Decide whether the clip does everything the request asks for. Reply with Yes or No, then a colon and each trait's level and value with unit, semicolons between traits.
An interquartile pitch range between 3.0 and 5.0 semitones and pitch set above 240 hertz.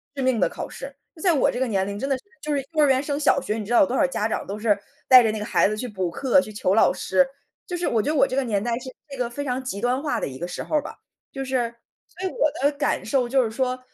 Yes: average, 4.1 semitones; very high, 255 Hz